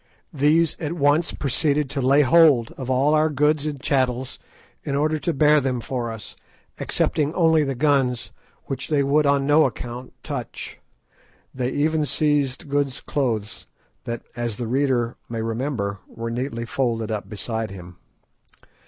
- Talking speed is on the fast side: No, average, 155 wpm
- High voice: No, low, 135 Hz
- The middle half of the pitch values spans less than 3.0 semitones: No, average, 3.8 semitones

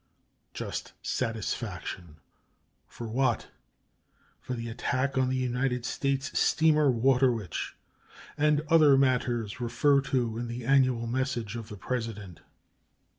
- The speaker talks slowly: Yes, slow, 120 wpm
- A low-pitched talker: Yes, low, 125 Hz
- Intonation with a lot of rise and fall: No, average, 2.8 semitones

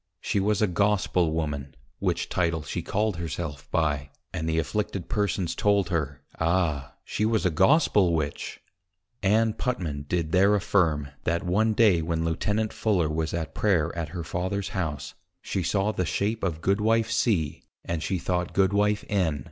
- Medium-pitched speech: No, very low, 90 Hz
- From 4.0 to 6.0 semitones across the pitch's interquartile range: Yes, average, 4.4 semitones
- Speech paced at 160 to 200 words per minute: Yes, average, 170 wpm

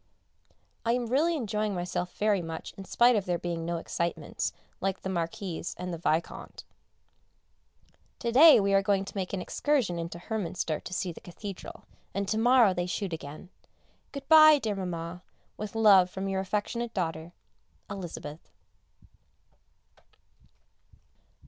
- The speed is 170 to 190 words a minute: No, average, 145 wpm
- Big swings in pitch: No, average, 4.1 semitones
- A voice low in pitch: No, high, 195 Hz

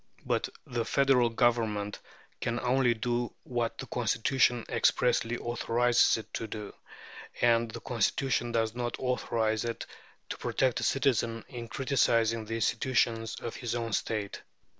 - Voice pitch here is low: Yes, low, 120 Hz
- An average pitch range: No, narrow, 1.4 semitones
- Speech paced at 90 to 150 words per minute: Yes, average, 140 wpm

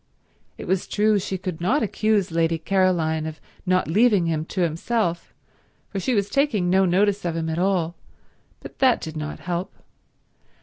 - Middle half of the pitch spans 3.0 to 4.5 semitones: Yes, average, 3.6 semitones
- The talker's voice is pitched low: No, medium, 185 Hz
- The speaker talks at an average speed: Yes, average, 170 wpm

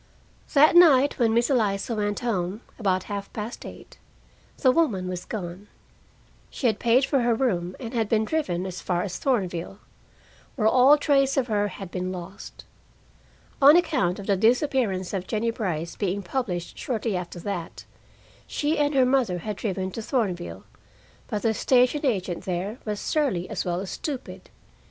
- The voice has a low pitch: No, high, 215 Hz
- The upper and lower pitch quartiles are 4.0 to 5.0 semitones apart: No, wide, 5.5 semitones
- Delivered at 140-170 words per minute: Yes, average, 165 wpm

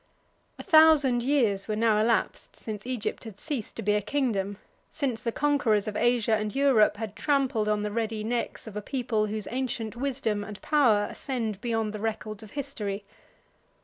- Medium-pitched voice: No, high, 225 Hz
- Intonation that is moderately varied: Yes, average, 3.3 semitones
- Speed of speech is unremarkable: Yes, average, 180 wpm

